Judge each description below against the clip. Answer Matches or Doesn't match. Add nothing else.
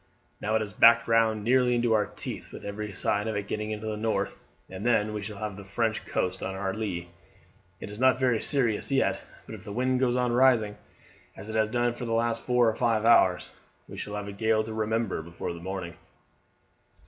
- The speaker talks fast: Matches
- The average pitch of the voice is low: Matches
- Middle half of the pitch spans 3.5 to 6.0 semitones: Doesn't match